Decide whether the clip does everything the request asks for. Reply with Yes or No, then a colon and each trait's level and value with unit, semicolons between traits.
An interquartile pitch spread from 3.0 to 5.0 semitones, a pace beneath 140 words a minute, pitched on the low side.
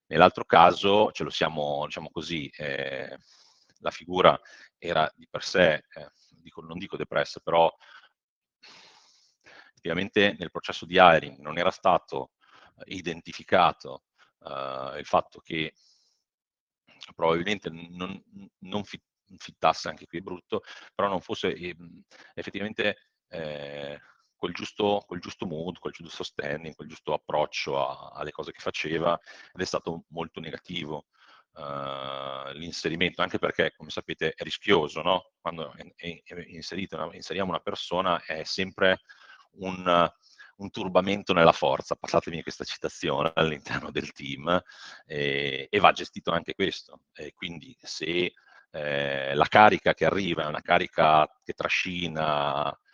Yes: average, 4.4 semitones; average, 130 wpm; very low, 80 Hz